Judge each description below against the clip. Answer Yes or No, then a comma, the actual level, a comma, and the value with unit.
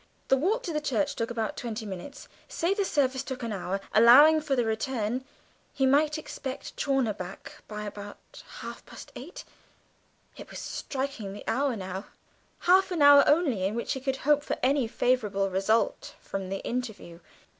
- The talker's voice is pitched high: Yes, very high, 250 Hz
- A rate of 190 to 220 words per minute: No, average, 165 wpm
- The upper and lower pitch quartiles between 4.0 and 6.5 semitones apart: Yes, average, 5.3 semitones